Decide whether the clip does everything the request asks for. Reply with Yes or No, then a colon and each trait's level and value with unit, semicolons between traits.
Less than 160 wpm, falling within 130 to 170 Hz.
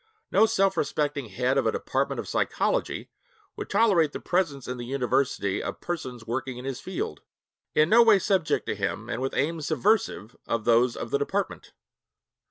No: average, 180 wpm; medium, 140 Hz